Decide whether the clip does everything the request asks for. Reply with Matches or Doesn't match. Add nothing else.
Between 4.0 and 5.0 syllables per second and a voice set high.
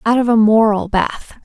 Matches